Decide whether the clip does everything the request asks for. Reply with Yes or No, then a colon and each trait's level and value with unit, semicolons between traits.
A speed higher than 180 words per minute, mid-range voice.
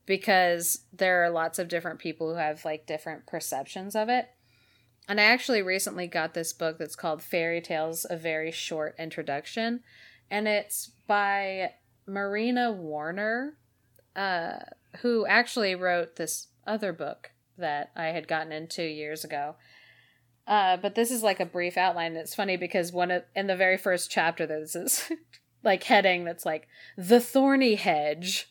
No: average, 160 wpm; medium, 175 Hz